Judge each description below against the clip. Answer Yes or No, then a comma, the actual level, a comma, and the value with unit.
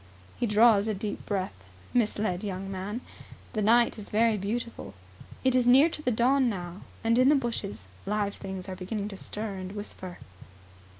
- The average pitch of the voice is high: Yes, high, 210 Hz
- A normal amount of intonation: Yes, average, 3.6 semitones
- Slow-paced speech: No, average, 175 wpm